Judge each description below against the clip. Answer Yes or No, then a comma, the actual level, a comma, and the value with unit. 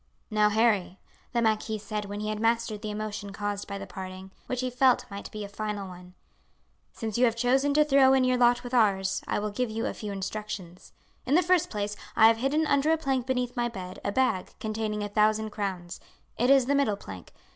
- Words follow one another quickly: Yes, fast, 220 wpm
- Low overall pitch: No, high, 215 Hz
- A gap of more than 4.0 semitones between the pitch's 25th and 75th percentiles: No, average, 3.6 semitones